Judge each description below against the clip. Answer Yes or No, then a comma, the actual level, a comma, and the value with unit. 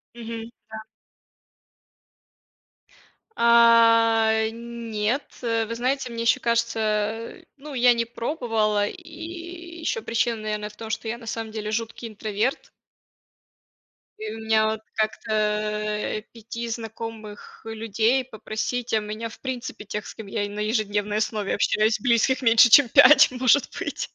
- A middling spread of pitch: No, narrow, 1.6 semitones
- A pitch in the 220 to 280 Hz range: Yes, high, 225 Hz